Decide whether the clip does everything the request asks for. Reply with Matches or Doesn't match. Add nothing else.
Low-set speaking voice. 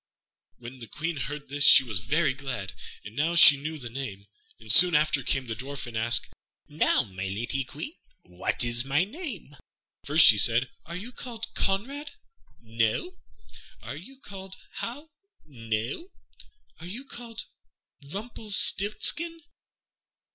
Doesn't match